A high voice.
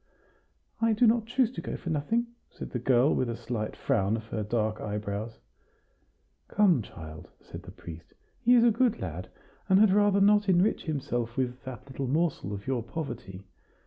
No: low, 130 Hz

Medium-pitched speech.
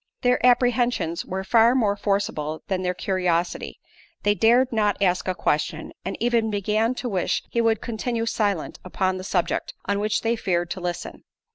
No: high, 205 Hz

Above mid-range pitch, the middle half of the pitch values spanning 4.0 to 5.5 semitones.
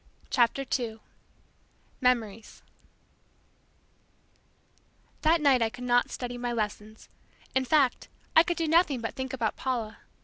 No: high, 245 Hz; average, 3.2 semitones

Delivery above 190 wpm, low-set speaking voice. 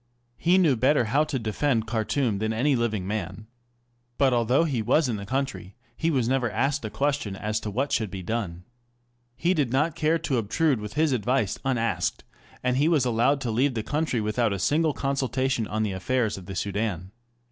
Yes: average, 200 wpm; low, 120 Hz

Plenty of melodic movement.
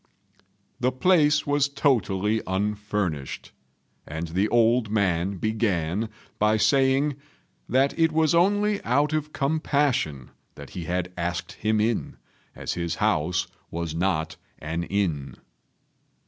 Yes: wide, 8.1 semitones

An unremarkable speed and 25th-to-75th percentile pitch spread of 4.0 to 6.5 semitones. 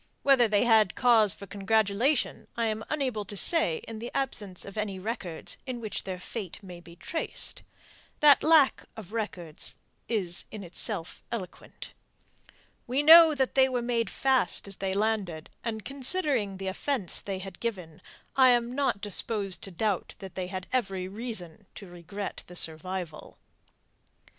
Yes: average, 155 wpm; average, 4.5 semitones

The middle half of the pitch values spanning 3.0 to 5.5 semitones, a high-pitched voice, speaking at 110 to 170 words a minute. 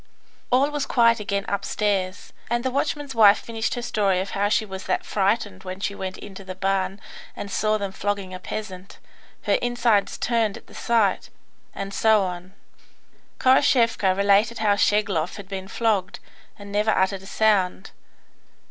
No: narrow, 2.6 semitones; high, 205 Hz; average, 165 wpm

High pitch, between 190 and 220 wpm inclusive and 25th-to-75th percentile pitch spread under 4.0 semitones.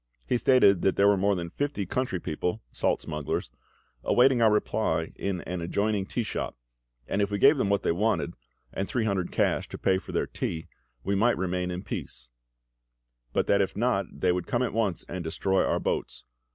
No: low, 100 Hz; average, 200 wpm; average, 3.6 semitones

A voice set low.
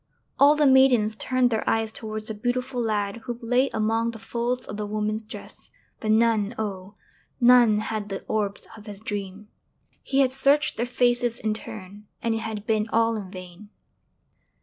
No: high, 220 Hz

